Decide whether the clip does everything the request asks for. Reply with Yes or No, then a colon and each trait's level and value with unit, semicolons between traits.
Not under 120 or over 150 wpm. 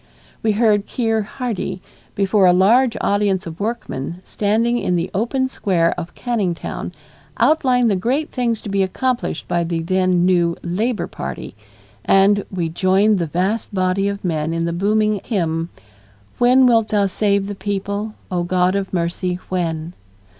No: average, 160 wpm